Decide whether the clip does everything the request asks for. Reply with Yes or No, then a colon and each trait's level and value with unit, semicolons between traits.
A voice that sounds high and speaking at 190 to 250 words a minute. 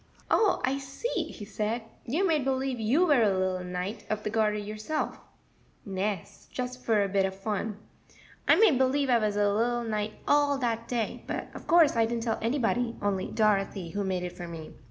Yes: high, 220 Hz; average, 195 wpm